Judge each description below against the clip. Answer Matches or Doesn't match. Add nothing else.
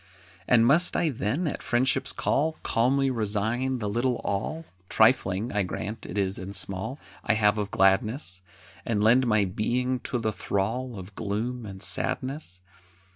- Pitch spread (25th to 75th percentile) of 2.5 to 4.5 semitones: Matches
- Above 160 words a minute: Doesn't match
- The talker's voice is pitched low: Matches